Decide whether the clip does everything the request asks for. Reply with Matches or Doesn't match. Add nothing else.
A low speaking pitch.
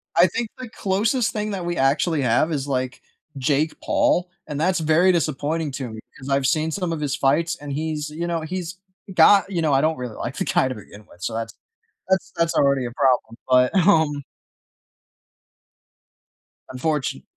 Doesn't match